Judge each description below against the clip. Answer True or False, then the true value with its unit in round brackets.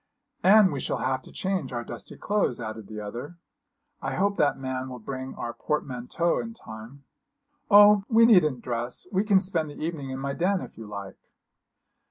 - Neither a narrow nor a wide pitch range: False (7.7 semitones)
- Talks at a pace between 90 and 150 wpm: False (185 wpm)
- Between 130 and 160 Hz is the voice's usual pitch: True (140 Hz)